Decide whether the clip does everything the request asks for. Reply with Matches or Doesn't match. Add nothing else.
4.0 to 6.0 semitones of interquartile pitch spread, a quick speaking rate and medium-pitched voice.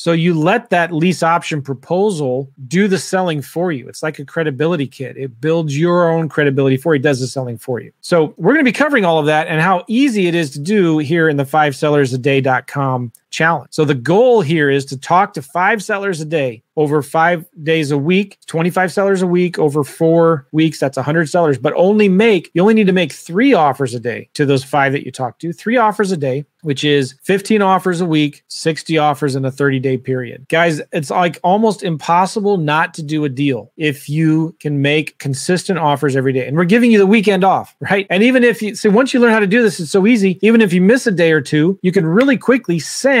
Matches